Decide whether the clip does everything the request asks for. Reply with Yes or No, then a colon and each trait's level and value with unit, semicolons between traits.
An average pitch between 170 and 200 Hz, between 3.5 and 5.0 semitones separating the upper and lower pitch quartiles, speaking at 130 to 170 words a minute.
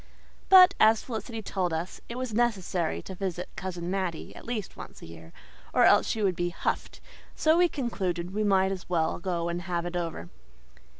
No: medium, 185 Hz; average, 4.0 semitones; average, 190 wpm